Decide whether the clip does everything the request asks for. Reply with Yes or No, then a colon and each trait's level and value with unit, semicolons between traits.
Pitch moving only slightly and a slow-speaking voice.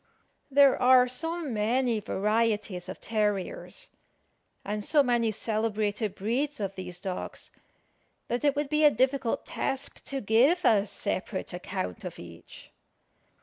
No: average, 4.9 semitones; slow, 130 wpm